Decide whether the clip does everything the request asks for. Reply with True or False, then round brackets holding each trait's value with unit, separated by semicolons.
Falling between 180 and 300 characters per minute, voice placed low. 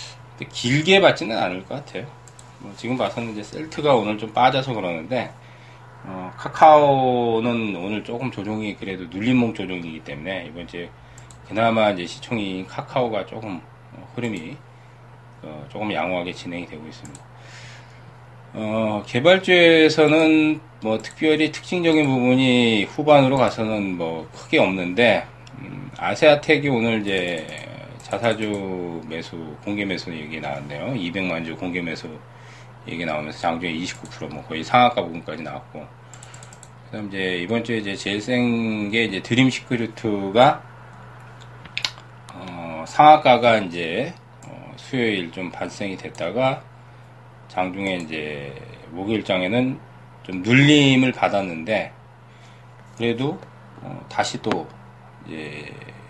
True (265 characters per minute; 115 Hz)